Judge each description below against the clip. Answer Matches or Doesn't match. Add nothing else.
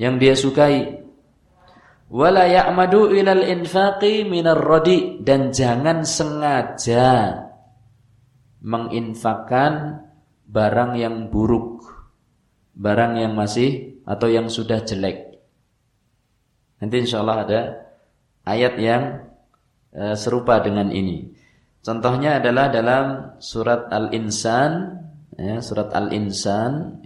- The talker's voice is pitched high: Doesn't match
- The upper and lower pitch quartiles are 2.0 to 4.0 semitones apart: Doesn't match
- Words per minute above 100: Doesn't match